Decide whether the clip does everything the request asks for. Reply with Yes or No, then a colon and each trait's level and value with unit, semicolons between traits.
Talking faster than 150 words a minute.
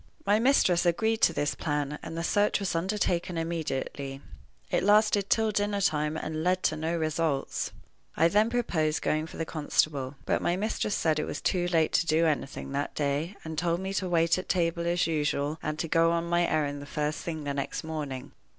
Yes: fast, 205 wpm